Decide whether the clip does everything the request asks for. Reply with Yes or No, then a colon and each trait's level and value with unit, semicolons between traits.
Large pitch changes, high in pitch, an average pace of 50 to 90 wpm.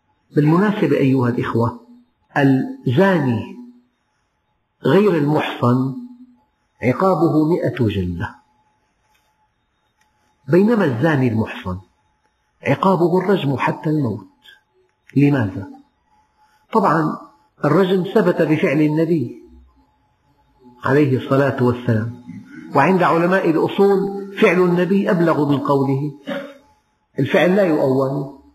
No: wide, 7.3 semitones; medium, 150 Hz; average, 75 wpm